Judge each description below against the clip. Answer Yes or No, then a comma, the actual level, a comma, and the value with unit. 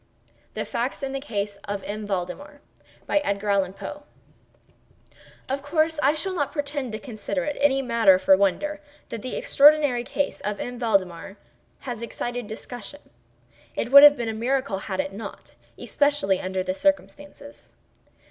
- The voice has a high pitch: Yes, high, 245 Hz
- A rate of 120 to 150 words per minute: Yes, average, 140 wpm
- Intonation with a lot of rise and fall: Yes, wide, 6.2 semitones